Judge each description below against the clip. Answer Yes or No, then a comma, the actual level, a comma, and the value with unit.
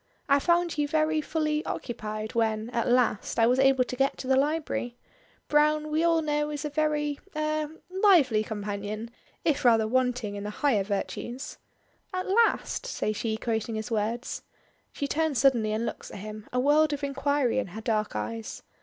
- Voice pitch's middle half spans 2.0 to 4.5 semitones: No, wide, 5.6 semitones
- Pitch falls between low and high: No, very high, 260 Hz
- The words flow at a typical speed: Yes, average, 180 wpm